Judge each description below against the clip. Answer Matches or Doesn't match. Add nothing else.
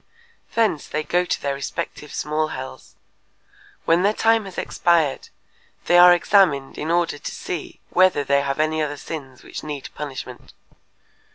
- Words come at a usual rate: Matches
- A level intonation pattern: Doesn't match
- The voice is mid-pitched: Matches